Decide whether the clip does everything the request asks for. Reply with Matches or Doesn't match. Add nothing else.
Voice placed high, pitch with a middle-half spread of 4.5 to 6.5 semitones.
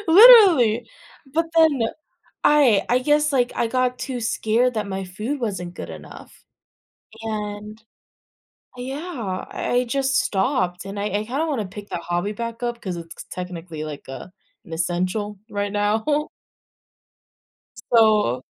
Matches